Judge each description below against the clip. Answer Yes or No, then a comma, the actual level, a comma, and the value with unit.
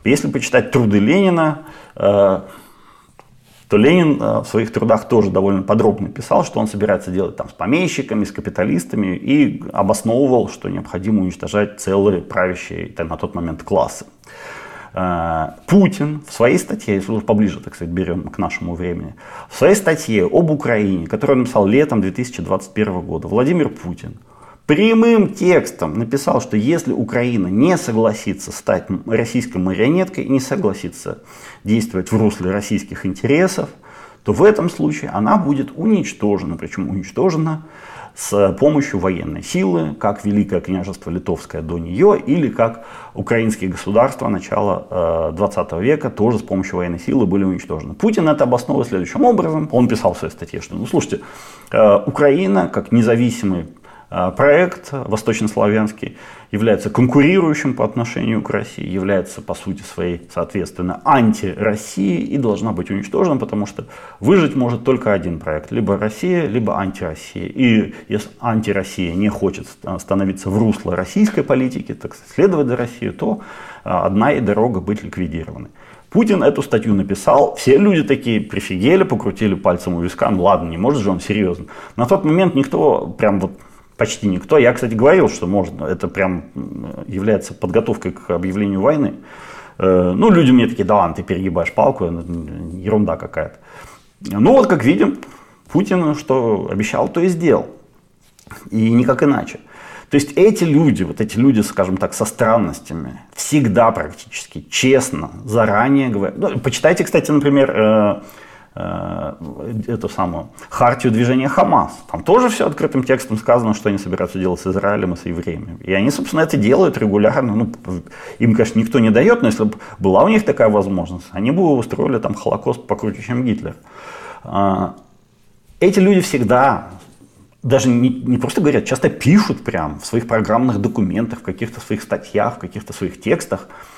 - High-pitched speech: No, low, 110 Hz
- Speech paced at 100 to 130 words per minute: No, average, 145 wpm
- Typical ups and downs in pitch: No, wide, 6.0 semitones